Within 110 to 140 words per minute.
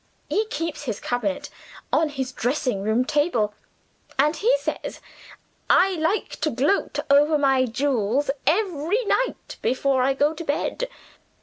Yes: slow, 135 wpm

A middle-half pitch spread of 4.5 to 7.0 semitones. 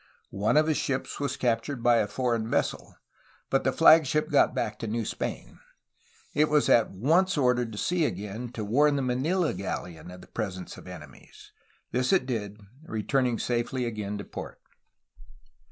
Yes: average, 5.0 semitones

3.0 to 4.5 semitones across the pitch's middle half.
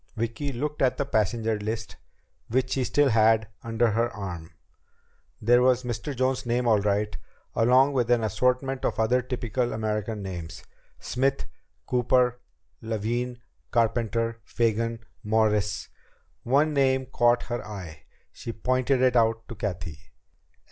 No: narrow, 2.6 semitones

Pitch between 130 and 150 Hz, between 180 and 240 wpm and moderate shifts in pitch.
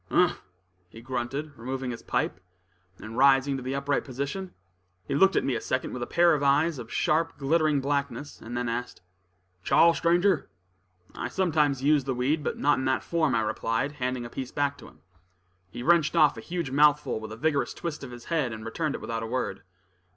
Yes: medium, 140 Hz; average, 200 wpm; average, 3.7 semitones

